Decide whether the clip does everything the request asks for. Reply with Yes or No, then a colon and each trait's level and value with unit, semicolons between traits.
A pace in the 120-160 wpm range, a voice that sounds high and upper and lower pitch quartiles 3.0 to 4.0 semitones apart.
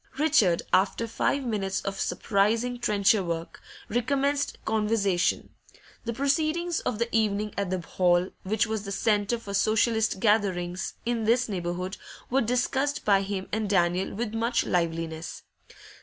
Yes: average, 140 wpm; high, 210 Hz; average, 3.6 semitones